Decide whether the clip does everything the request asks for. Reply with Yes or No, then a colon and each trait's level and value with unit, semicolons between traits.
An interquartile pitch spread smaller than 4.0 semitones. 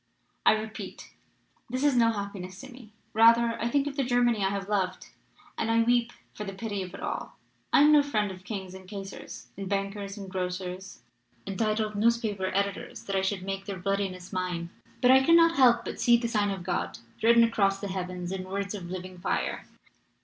Yes: average, 3.5 semitones